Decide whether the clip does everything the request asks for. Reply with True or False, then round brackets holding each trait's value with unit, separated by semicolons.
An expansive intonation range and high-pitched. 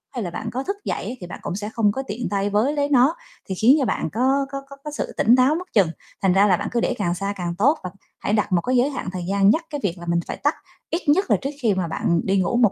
True (6.1 semitones; 220 Hz)